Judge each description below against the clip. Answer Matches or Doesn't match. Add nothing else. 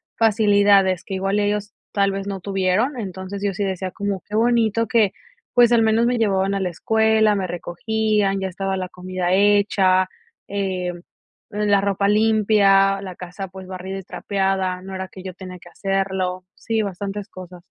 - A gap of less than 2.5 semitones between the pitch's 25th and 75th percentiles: Matches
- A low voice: Doesn't match